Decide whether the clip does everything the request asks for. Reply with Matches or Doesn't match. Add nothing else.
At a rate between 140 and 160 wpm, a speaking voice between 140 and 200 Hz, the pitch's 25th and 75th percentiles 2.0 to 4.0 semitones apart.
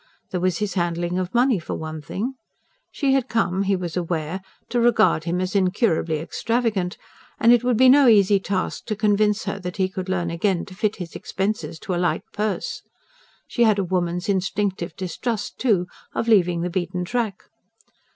Doesn't match